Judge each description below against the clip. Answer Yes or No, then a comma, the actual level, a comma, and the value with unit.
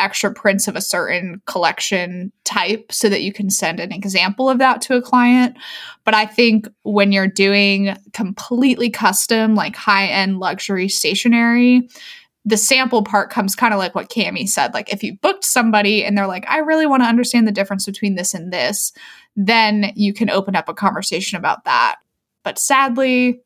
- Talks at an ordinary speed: Yes, average, 180 wpm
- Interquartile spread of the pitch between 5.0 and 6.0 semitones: No, average, 3.6 semitones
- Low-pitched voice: No, high, 210 Hz